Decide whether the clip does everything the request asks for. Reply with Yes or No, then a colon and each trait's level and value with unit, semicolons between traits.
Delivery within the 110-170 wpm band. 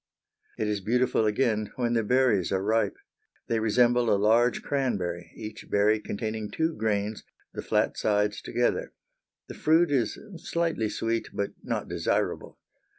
Yes: average, 145 wpm